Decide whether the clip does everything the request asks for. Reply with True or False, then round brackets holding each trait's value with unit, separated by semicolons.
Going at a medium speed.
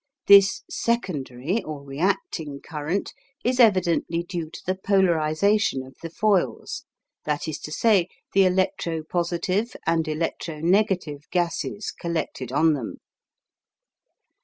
False (115 wpm)